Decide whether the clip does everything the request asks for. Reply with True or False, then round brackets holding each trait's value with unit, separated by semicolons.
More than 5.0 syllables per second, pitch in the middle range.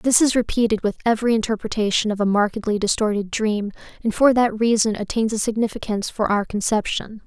False (6.1 syllables/s; 215 Hz)